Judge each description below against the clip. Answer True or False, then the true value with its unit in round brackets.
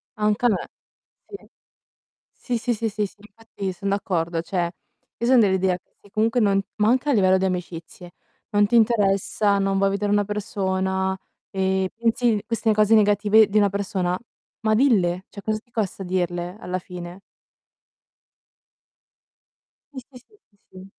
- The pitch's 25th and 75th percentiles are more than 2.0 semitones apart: True (2.4 semitones)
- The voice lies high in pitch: True (200 Hz)